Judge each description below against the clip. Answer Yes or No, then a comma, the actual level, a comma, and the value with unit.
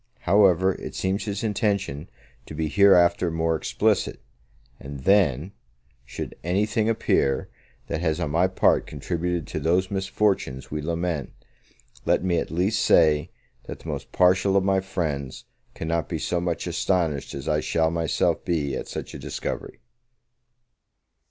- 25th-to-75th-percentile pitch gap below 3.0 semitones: No, average, 3.6 semitones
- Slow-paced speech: No, average, 145 wpm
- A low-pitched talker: Yes, very low, 85 Hz